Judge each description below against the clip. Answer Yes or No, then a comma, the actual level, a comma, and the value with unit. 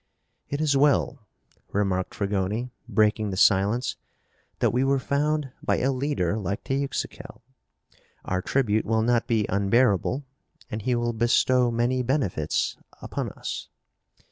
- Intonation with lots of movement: No, average, 4.6 semitones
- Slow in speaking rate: Yes, slow, 130 wpm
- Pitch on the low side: Yes, low, 120 Hz